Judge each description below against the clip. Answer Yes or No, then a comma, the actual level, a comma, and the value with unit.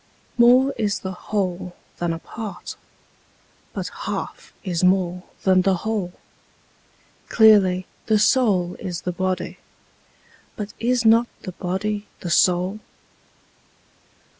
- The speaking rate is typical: No, slow, 115 wpm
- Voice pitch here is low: No, high, 190 Hz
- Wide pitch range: No, average, 3.2 semitones